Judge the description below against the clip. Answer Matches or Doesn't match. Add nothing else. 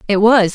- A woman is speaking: Matches